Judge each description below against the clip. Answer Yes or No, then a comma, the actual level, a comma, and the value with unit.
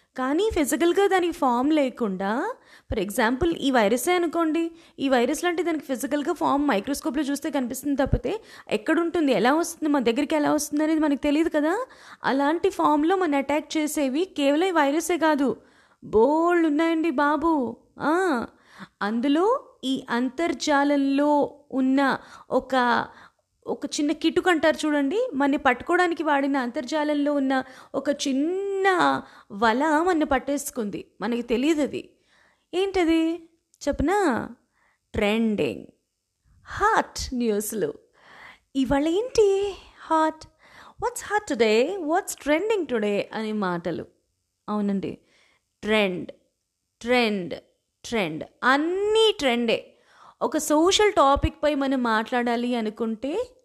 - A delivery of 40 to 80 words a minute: No, average, 105 wpm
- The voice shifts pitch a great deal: No, average, 4.7 semitones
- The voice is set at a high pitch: Yes, very high, 295 Hz